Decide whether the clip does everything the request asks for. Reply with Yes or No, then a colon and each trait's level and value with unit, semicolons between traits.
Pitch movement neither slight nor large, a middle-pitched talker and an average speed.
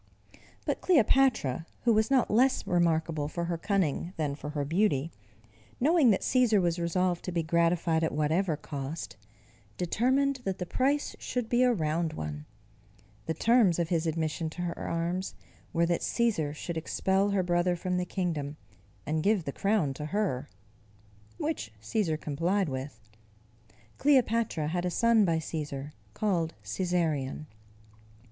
Yes: average, 4.8 semitones; medium, 175 Hz; average, 150 wpm